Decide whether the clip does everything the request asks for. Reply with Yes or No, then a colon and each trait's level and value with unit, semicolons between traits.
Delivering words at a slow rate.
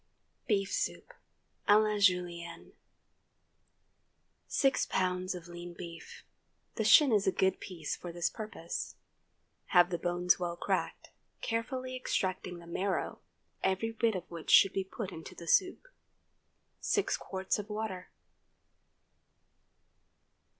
Yes: slow, 125 wpm